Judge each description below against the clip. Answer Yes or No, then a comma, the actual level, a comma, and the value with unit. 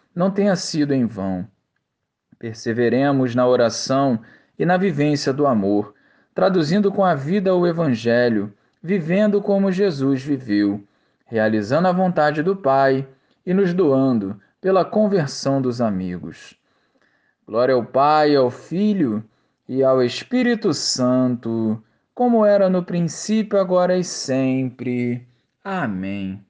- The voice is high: No, low, 135 Hz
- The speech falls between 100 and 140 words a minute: Yes, slow, 120 wpm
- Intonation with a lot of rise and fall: Yes, wide, 7.7 semitones